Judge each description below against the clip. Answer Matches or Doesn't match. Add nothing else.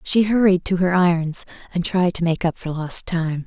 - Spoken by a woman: Matches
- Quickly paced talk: Matches